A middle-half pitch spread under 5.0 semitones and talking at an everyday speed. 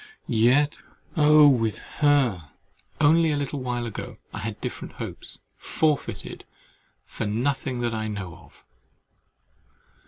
No: average, 4.5 semitones; slow, 120 wpm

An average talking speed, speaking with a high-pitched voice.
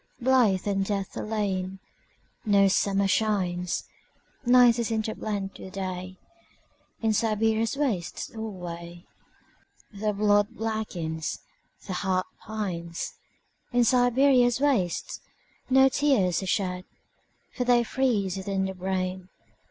No: slow, 85 wpm; high, 205 Hz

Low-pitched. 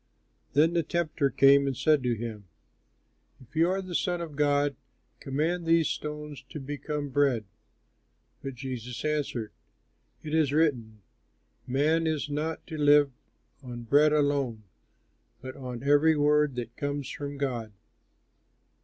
No: medium, 145 Hz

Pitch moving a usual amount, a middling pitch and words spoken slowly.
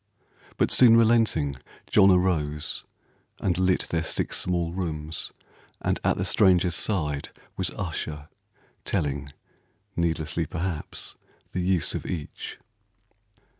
No: average, 3.5 semitones; very low, 85 Hz; slow, 110 wpm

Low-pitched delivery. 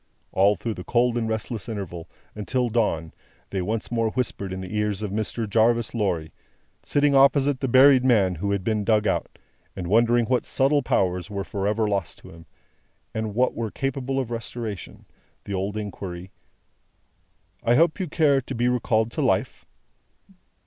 Yes: low, 110 Hz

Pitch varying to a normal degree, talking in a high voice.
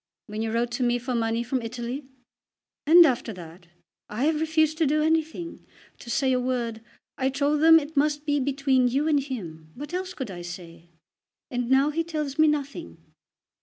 Yes: average, 4.4 semitones; very high, 270 Hz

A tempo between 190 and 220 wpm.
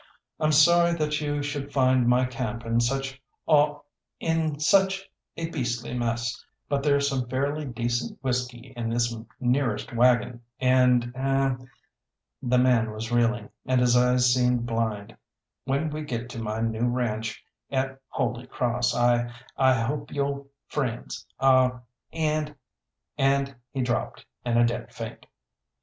No: average, 145 wpm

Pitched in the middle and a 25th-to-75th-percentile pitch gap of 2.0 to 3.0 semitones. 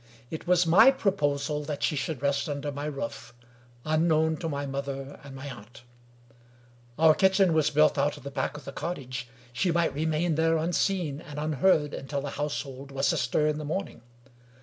Yes: medium, 150 Hz; narrow, 2.5 semitones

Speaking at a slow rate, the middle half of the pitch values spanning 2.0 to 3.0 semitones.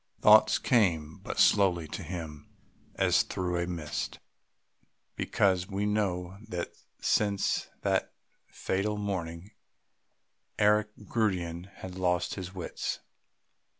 Yes: slow, 105 wpm; average, 2.7 semitones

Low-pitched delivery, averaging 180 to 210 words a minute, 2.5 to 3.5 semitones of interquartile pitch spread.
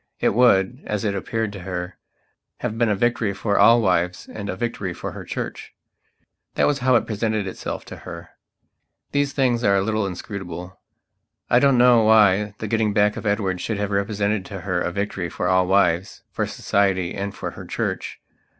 Yes: low, 100 Hz; average, 190 wpm; average, 3.0 semitones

